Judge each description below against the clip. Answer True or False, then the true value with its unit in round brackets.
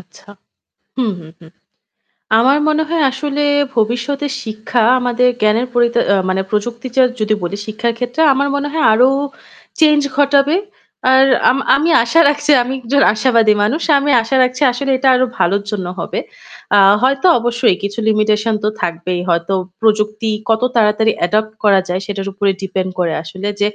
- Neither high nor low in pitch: False (230 Hz)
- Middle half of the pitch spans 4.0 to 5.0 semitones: True (4.3 semitones)